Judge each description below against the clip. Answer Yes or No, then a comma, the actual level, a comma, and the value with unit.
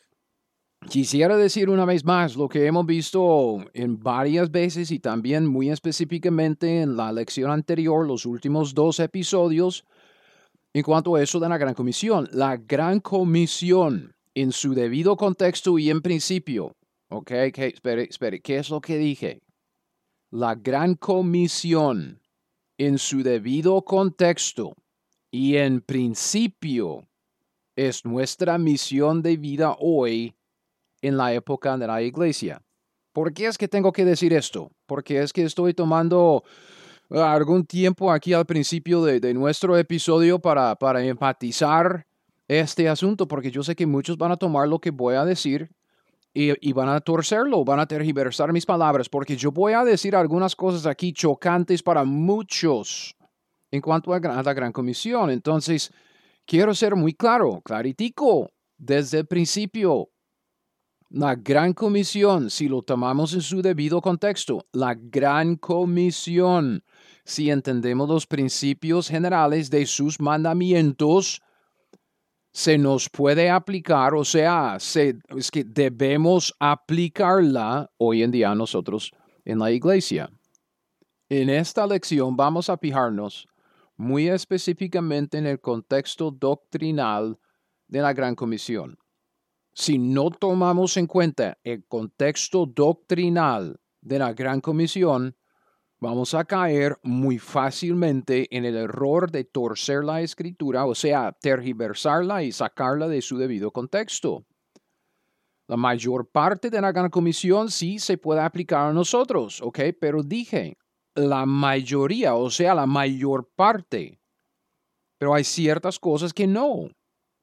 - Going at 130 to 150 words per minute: Yes, average, 135 wpm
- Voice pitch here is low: No, medium, 155 Hz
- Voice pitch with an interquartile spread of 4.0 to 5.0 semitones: Yes, average, 4.5 semitones